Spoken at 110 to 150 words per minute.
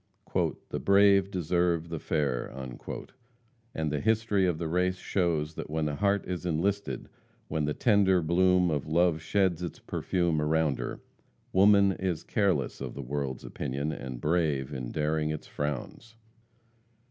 Yes: average, 145 wpm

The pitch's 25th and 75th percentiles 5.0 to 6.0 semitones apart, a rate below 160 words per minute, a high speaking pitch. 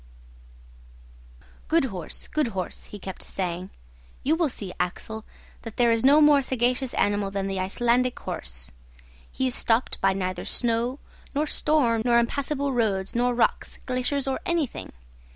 Yes: wide, 5.4 semitones; average, 150 wpm; high, 235 Hz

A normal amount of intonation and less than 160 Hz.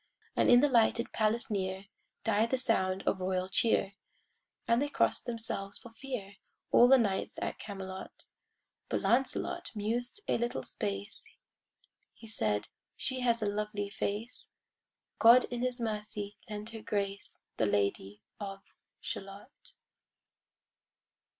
No: average, 3.4 semitones; high, 210 Hz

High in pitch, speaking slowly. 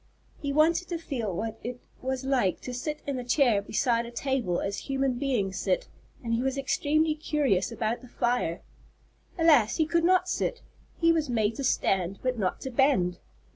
No: very high, 255 Hz; average, 185 wpm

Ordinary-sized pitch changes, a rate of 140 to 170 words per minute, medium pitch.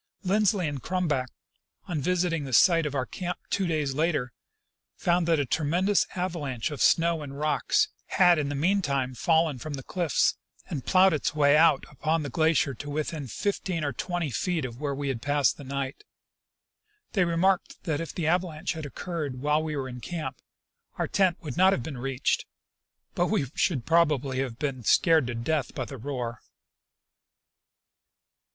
No: average, 4.0 semitones; average, 180 wpm; medium, 150 Hz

